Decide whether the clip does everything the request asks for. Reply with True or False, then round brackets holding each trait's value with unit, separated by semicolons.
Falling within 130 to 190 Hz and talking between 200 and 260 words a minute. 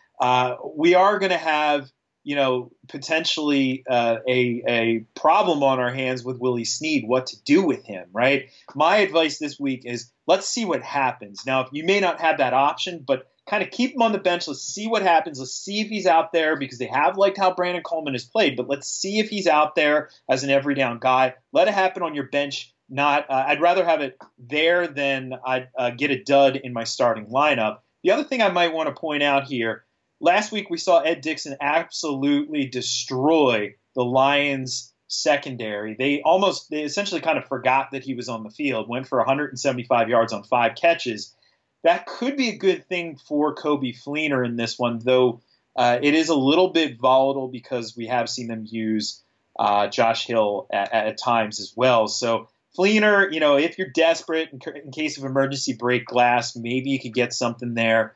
True (140 Hz; 205 wpm)